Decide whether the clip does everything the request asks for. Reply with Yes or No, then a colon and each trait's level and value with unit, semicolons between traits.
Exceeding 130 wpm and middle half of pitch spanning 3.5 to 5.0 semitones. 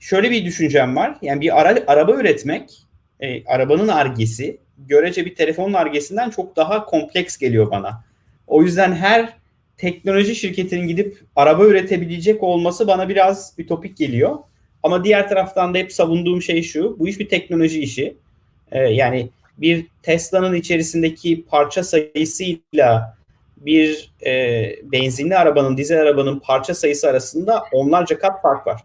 Yes: fast, 140 wpm; average, 4.6 semitones